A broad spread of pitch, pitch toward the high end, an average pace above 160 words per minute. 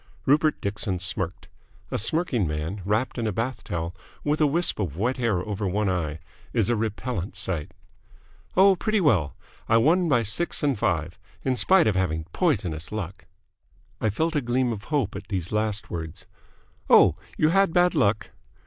No: wide, 7.4 semitones; low, 110 Hz; average, 175 wpm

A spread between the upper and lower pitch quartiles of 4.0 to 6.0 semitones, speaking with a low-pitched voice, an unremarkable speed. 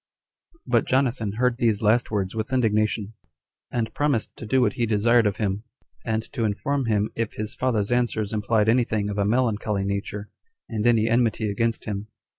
No: narrow, 2.4 semitones; low, 110 Hz; average, 185 wpm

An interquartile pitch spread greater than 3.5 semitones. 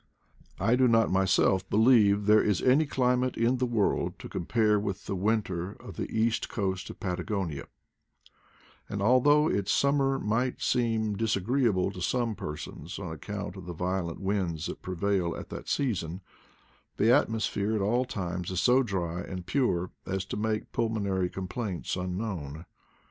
Yes: average, 4.0 semitones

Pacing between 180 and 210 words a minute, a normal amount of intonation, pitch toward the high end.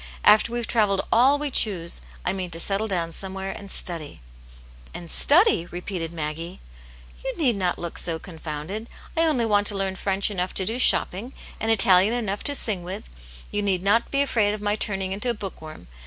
Yes: average, 200 wpm; average, 4.0 semitones; high, 195 Hz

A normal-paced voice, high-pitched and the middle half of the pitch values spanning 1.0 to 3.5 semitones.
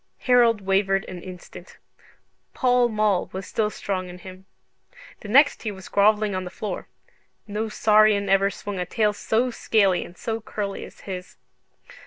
Yes: average, 160 wpm; high, 205 Hz; narrow, 2.4 semitones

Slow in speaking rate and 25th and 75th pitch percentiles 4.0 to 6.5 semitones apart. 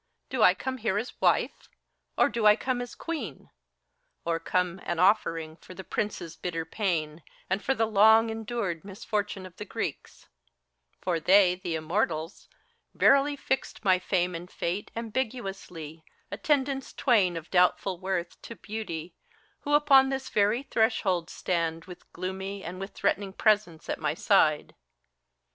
No: average, 155 wpm; average, 4.4 semitones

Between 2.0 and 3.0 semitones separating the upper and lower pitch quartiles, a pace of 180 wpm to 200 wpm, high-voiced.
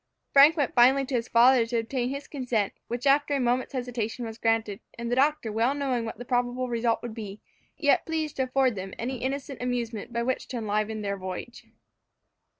Yes: average, 2.7 semitones; average, 195 wpm; high, 245 Hz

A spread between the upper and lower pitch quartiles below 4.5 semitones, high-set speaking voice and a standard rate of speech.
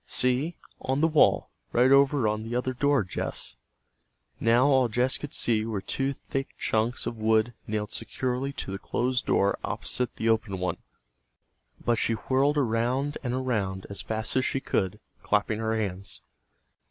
No: average, 3.3 semitones; low, 120 Hz; average, 165 wpm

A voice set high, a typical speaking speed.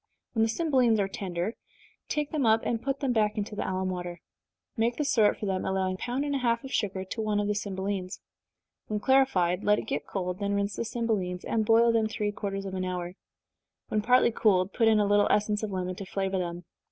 No: high, 210 Hz; fast, 230 wpm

